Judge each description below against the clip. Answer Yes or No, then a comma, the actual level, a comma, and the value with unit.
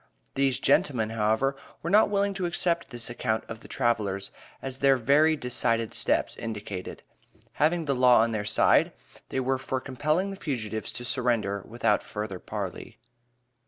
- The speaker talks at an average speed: Yes, average, 160 wpm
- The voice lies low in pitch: Yes, low, 125 Hz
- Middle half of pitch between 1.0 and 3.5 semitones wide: No, average, 4.3 semitones